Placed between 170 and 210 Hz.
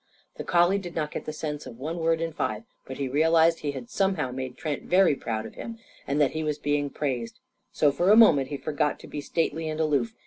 No: medium, 150 Hz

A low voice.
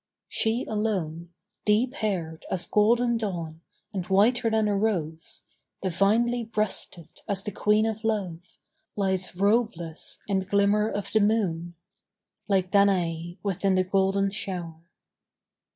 No: high, 200 Hz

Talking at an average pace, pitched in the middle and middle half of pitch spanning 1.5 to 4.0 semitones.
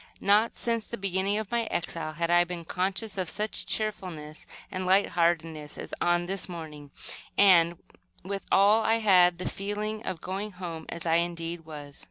Yes: average, 175 wpm; medium, 180 Hz; average, 3.3 semitones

